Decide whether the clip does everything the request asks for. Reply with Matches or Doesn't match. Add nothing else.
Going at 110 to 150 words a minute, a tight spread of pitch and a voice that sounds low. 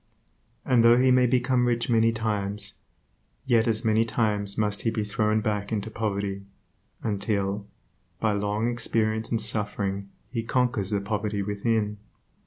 Matches